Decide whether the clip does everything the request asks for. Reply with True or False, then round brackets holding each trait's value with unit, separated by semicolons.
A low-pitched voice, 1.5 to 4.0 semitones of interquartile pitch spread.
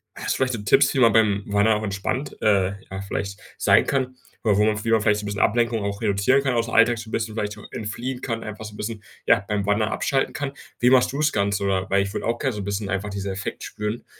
True (105 Hz; 2.7 semitones)